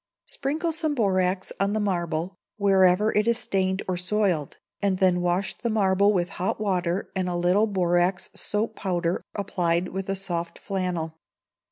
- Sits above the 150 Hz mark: Yes, high, 190 Hz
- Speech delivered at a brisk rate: No, average, 160 wpm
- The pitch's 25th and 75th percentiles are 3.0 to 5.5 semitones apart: No, narrow, 2.4 semitones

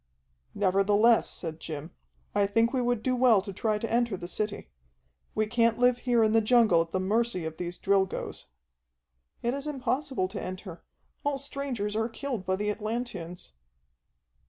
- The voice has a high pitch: Yes, high, 215 Hz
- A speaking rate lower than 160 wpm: No, average, 165 wpm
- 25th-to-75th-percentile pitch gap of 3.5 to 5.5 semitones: Yes, average, 4.3 semitones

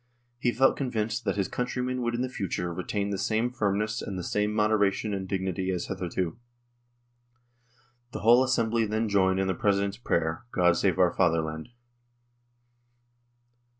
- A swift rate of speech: No, average, 160 wpm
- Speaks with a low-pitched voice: Yes, low, 105 Hz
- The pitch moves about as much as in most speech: Yes, average, 3.6 semitones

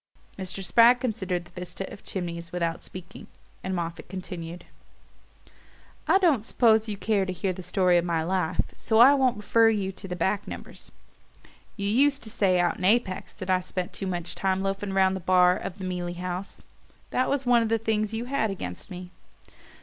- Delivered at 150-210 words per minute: Yes, average, 195 wpm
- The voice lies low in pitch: No, high, 190 Hz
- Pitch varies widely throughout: No, average, 3.6 semitones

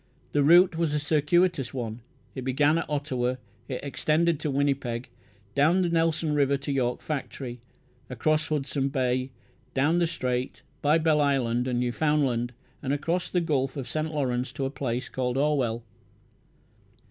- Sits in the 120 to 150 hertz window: Yes, medium, 140 Hz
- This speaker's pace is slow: No, average, 155 wpm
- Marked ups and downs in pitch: No, average, 3.3 semitones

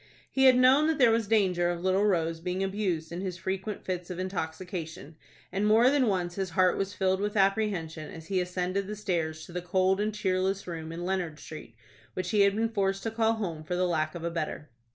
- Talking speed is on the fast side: Yes, fast, 225 wpm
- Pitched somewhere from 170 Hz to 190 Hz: Yes, medium, 185 Hz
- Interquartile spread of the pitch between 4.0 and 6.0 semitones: No, average, 3.0 semitones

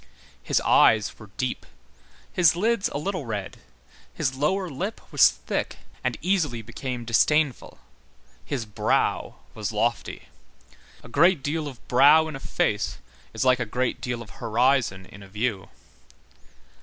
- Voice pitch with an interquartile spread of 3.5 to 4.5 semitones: No, wide, 5.4 semitones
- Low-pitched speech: Yes, low, 130 Hz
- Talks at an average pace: Yes, average, 145 wpm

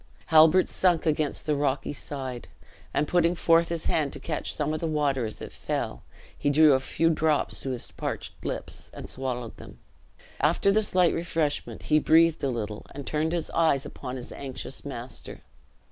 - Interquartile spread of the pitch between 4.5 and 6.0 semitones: No, average, 3.4 semitones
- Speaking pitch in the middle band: Yes, medium, 150 Hz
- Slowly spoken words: No, average, 175 wpm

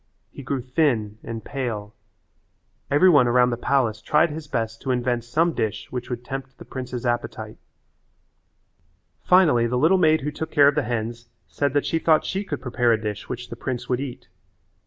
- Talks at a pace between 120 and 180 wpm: No, average, 190 wpm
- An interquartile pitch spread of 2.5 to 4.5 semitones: Yes, average, 3.6 semitones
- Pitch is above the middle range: No, low, 125 Hz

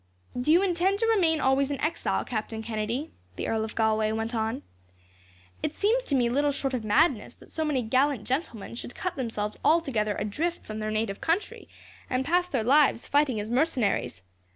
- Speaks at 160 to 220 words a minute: Yes, average, 185 wpm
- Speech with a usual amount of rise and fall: No, wide, 6.1 semitones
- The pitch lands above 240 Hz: Yes, very high, 260 Hz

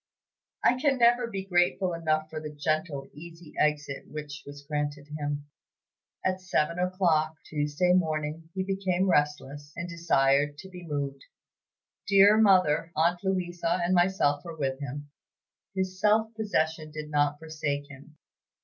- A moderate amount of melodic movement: Yes, average, 3.9 semitones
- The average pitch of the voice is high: No, medium, 160 Hz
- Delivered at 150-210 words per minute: No, average, 140 wpm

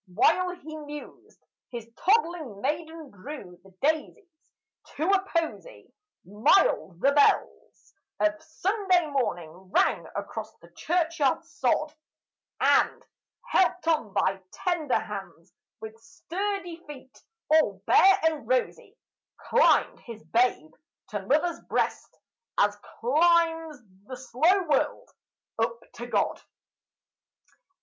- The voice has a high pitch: Yes, very high, 305 Hz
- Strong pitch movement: Yes, wide, 7.1 semitones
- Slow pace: Yes, slow, 110 wpm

